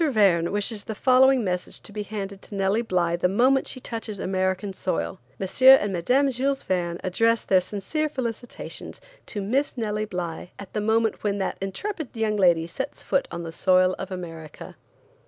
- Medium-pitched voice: No, high, 205 Hz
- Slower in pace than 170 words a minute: No, average, 175 wpm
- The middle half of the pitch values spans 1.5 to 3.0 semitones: No, average, 4.5 semitones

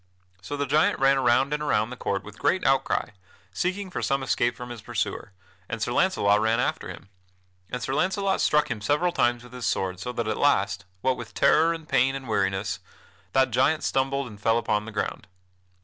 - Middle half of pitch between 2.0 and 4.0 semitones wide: No, average, 4.6 semitones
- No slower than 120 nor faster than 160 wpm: No, fast, 205 wpm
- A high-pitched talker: No, low, 125 Hz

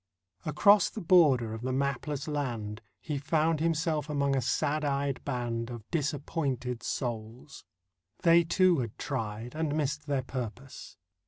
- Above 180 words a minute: No, average, 140 wpm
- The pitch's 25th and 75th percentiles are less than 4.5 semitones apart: Yes, average, 4.0 semitones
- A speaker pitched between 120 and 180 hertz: Yes, medium, 140 Hz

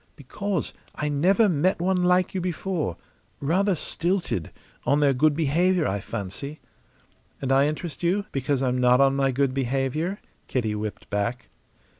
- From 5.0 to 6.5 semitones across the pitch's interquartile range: Yes, wide, 5.6 semitones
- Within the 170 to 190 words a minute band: No, average, 150 wpm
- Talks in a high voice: No, medium, 145 Hz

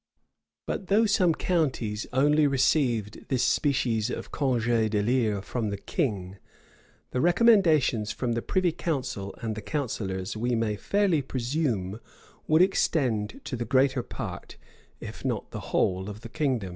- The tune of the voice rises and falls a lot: Yes, wide, 6.1 semitones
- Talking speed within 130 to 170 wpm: Yes, average, 145 wpm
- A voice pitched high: No, low, 125 Hz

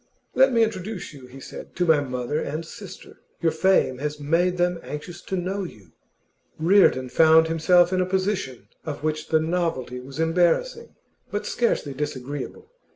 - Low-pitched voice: No, medium, 165 Hz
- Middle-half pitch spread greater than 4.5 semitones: No, average, 4.1 semitones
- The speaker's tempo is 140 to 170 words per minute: Yes, average, 160 wpm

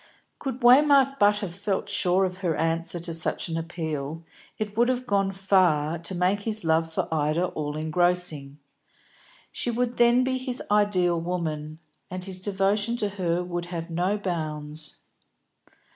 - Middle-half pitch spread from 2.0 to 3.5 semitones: No, average, 4.1 semitones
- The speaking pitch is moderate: Yes, medium, 180 Hz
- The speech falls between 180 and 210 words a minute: No, average, 160 wpm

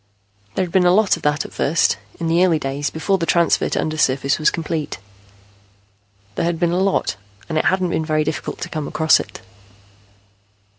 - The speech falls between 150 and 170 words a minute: No, average, 195 wpm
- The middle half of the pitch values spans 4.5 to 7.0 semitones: No, narrow, 2.4 semitones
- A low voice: No, medium, 165 Hz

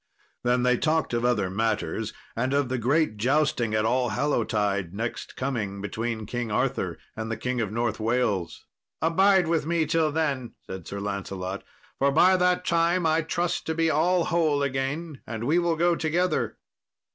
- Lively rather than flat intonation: Yes, wide, 6.5 semitones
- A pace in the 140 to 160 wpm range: No, average, 170 wpm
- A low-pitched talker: Yes, low, 130 Hz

